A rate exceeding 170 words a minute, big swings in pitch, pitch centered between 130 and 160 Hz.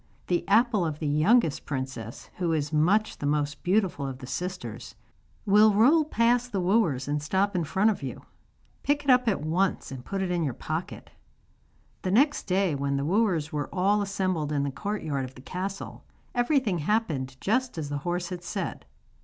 No: average, 185 wpm; wide, 6.2 semitones; medium, 180 Hz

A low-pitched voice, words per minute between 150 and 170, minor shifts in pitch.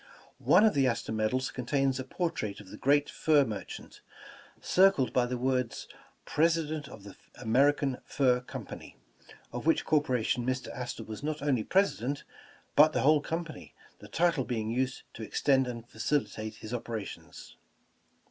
No: low, 130 Hz; average, 155 wpm; average, 4.0 semitones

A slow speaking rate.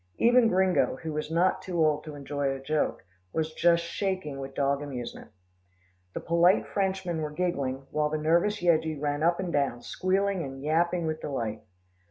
No: average, 175 wpm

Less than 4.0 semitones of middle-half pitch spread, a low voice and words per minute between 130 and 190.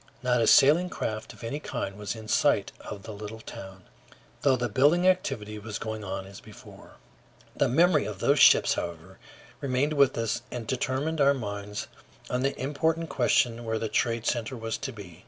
No: average, 4.8 semitones; low, 115 Hz; average, 185 wpm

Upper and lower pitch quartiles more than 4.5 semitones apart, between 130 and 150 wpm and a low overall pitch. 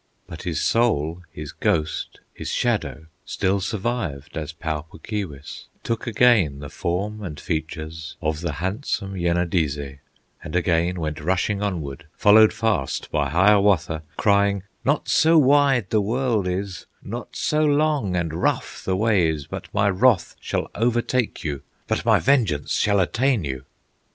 Yes: wide, 5.6 semitones; average, 145 wpm; very low, 95 Hz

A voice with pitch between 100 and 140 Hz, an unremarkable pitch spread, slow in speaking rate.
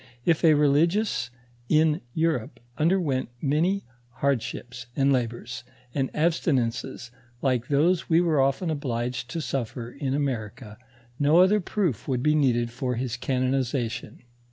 Yes: low, 135 Hz; average, 4.3 semitones; slow, 130 wpm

